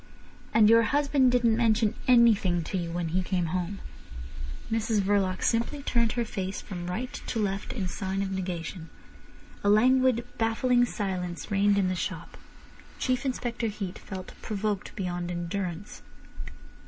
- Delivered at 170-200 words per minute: No, average, 145 wpm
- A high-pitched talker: Yes, high, 205 Hz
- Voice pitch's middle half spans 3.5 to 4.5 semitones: Yes, average, 4.0 semitones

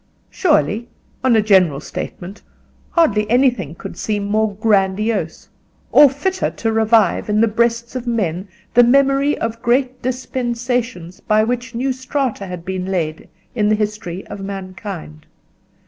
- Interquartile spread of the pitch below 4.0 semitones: No, average, 4.4 semitones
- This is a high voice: Yes, high, 220 Hz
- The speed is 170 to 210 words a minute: No, average, 140 wpm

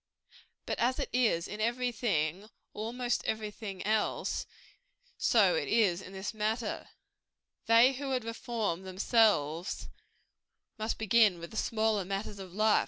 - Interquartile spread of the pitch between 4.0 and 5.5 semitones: No, average, 3.2 semitones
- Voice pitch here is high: Yes, high, 215 Hz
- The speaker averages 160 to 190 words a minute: No, average, 145 wpm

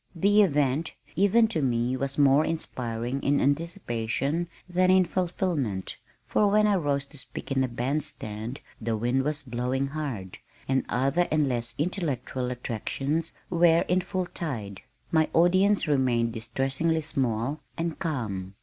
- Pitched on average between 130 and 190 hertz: Yes, medium, 140 Hz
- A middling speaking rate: Yes, average, 145 wpm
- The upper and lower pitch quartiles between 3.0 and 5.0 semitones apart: No, wide, 5.4 semitones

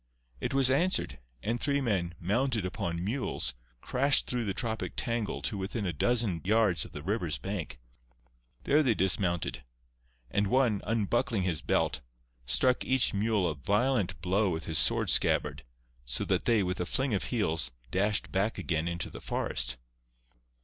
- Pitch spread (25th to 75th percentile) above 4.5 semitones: Yes, wide, 5.5 semitones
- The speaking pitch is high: No, low, 100 Hz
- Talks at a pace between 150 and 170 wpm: Yes, average, 160 wpm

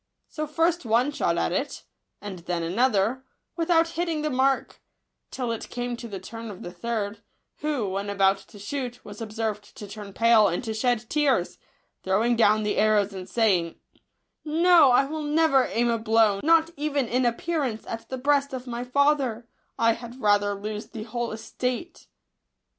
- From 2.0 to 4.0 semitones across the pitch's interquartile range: No, average, 4.7 semitones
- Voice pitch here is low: No, high, 235 Hz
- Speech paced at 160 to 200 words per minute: Yes, average, 175 wpm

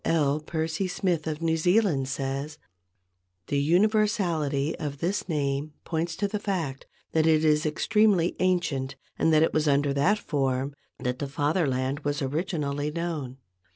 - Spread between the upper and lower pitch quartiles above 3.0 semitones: Yes, average, 3.6 semitones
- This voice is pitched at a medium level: Yes, medium, 155 Hz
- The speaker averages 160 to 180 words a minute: No, average, 145 wpm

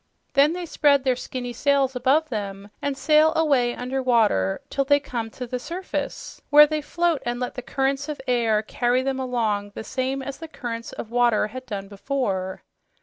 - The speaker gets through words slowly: No, average, 190 wpm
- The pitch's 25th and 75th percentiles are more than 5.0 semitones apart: No, average, 3.4 semitones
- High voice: Yes, very high, 255 Hz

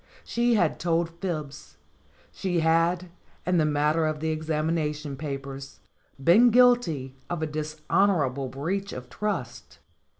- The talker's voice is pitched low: No, medium, 160 Hz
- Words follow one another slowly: Yes, slow, 125 wpm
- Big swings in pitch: No, average, 3.6 semitones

